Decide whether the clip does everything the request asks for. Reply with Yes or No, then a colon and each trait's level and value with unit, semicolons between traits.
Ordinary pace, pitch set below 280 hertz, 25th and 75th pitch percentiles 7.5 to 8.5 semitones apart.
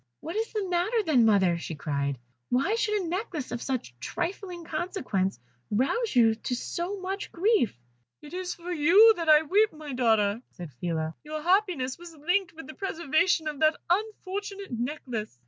No: average, 165 wpm; very high, 315 Hz; wide, 7.8 semitones